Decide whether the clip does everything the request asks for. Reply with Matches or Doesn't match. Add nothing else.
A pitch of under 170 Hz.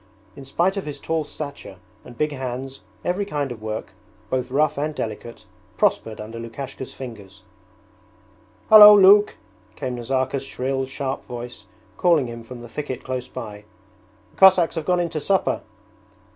Matches